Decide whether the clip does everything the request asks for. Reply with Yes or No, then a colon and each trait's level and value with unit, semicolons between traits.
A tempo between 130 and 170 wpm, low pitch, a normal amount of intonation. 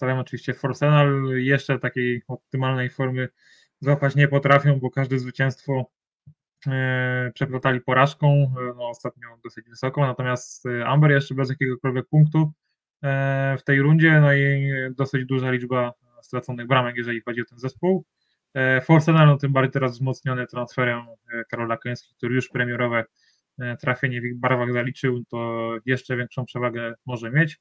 No: average, 135 wpm; low, 130 Hz; narrow, 2.0 semitones